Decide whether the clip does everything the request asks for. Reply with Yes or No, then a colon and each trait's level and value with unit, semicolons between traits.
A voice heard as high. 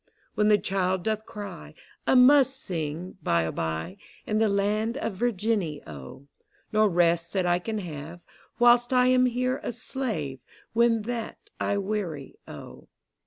Yes: high, 205 Hz